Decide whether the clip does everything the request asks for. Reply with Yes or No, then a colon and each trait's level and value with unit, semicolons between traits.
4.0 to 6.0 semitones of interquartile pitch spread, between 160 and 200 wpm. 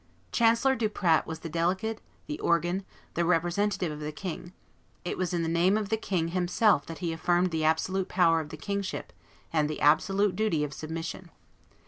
No: average, 3.4 semitones; average, 180 wpm